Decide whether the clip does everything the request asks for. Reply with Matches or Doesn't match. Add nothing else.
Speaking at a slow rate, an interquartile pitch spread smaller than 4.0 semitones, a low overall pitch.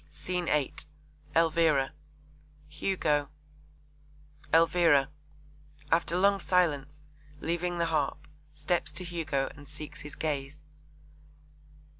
Doesn't match